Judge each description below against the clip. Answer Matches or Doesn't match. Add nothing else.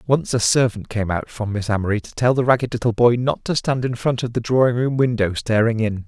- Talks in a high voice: Doesn't match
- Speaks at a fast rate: Matches